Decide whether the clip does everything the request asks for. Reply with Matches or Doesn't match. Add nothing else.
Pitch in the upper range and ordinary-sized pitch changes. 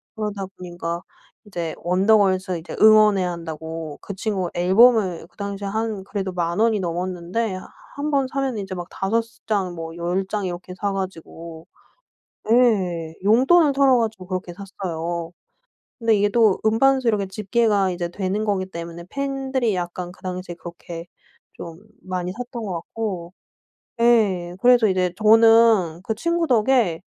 Matches